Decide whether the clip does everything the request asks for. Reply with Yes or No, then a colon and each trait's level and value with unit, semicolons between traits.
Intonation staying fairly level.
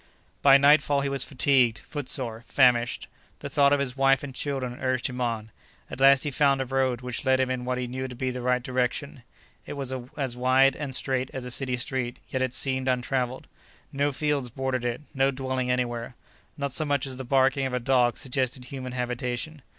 Yes: narrow, 1.6 semitones